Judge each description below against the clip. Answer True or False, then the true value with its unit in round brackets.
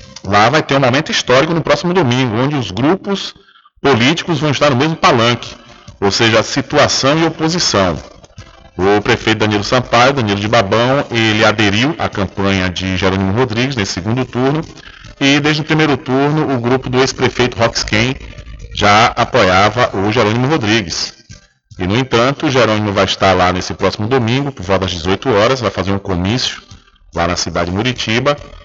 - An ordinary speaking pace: True (170 wpm)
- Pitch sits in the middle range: False (115 Hz)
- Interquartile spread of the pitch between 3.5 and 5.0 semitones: False (5.5 semitones)